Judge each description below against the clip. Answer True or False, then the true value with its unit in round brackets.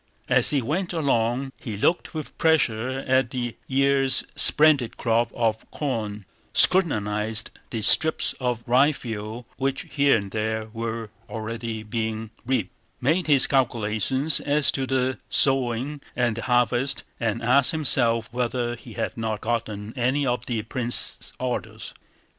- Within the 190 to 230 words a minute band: False (135 wpm)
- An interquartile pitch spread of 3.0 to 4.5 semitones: True (3.3 semitones)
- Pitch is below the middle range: True (120 Hz)